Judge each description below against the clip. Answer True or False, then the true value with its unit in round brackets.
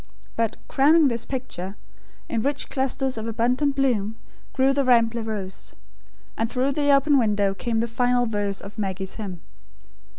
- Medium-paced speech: True (155 wpm)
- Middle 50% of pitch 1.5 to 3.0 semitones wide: False (4.2 semitones)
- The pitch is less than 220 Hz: False (235 Hz)